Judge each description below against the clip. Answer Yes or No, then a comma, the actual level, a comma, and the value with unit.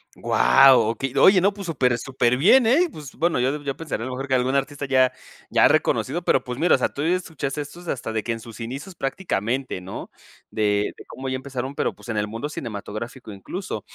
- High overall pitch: No, low, 130 Hz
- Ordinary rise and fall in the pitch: Yes, average, 4.1 semitones